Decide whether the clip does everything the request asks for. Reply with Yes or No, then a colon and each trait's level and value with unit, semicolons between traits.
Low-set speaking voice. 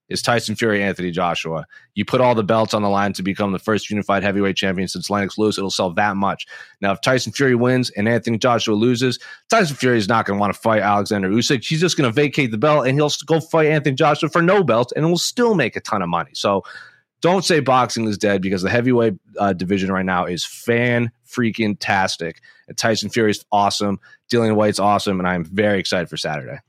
Yes: low, 110 Hz